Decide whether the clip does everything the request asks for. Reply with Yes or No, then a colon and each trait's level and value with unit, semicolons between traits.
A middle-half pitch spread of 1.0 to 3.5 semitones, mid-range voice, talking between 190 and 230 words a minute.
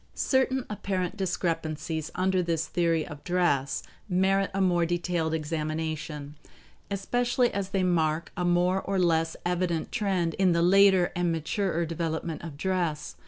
No: average, 2.8 semitones; medium, 175 Hz; average, 140 wpm